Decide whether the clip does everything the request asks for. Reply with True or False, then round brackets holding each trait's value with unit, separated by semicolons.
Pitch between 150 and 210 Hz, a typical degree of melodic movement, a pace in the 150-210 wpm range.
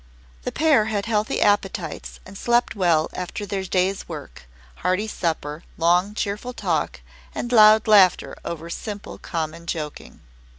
False (190 Hz; 4.0 semitones; 135 wpm)